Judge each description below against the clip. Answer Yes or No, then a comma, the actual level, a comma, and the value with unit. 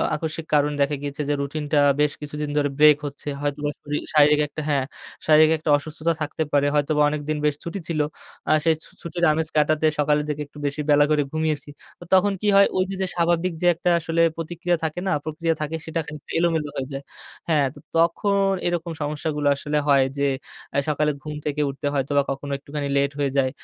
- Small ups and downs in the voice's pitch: Yes, narrow, 2.0 semitones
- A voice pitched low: No, medium, 150 Hz